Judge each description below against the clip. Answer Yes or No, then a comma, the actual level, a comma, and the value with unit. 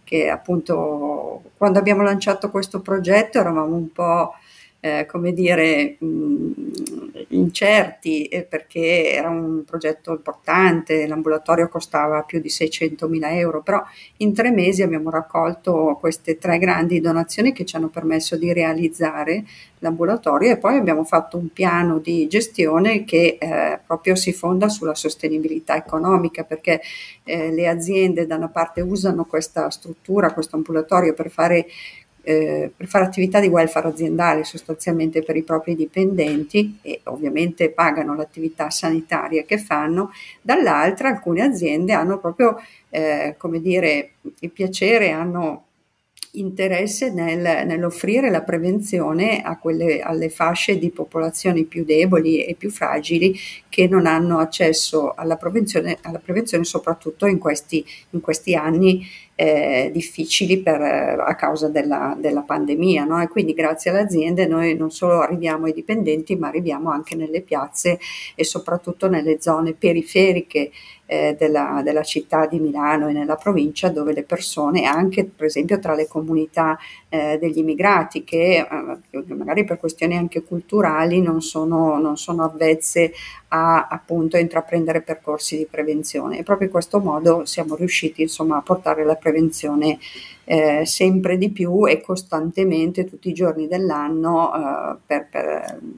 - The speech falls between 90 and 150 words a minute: Yes, average, 145 wpm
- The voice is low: No, medium, 165 Hz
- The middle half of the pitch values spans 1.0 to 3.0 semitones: Yes, narrow, 2.6 semitones